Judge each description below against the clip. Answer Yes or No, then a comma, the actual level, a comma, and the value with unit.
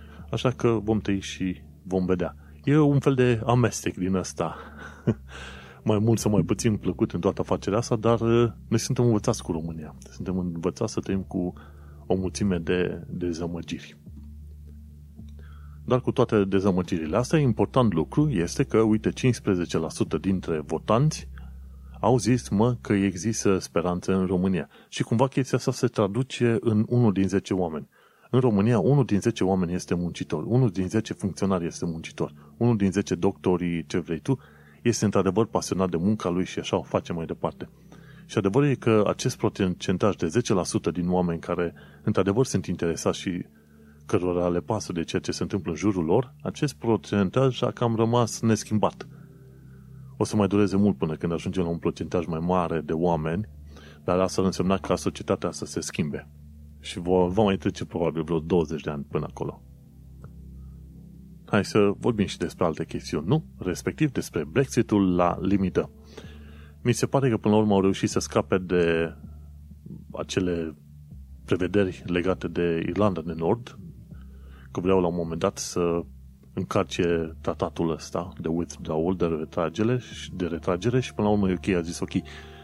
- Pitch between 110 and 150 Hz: No, very low, 95 Hz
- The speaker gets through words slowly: No, average, 165 wpm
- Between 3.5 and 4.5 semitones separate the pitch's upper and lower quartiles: No, average, 5.0 semitones